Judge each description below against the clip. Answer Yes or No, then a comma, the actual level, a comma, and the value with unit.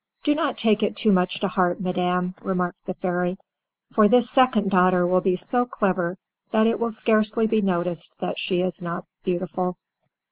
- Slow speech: No, average, 180 wpm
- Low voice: No, medium, 185 Hz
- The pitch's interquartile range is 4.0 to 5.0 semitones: No, average, 3.3 semitones